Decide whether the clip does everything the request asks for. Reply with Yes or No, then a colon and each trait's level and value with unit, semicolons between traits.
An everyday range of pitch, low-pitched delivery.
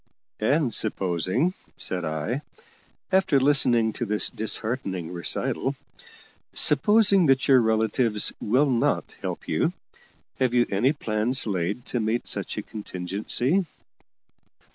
Yes: average, 4.6 semitones; low, 115 Hz